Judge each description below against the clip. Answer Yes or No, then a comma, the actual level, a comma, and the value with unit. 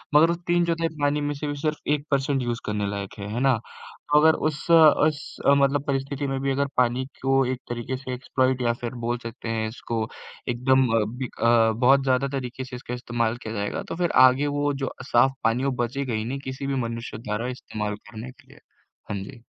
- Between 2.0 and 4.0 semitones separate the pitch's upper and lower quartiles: Yes, average, 3.0 semitones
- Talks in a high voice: No, low, 130 Hz